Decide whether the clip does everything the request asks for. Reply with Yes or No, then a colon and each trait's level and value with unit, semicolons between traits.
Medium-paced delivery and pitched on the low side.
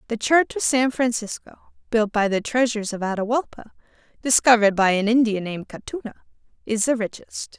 No: average, 160 wpm; high, 230 Hz